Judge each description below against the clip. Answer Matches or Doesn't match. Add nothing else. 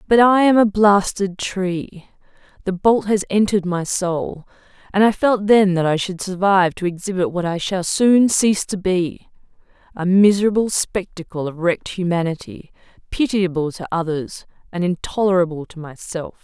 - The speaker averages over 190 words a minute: Doesn't match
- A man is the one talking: Doesn't match